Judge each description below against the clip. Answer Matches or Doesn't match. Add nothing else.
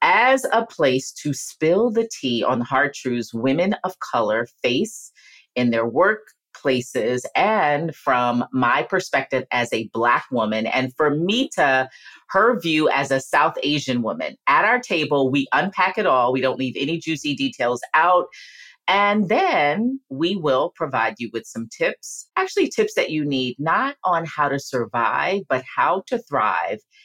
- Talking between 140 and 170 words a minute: Matches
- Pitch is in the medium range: Matches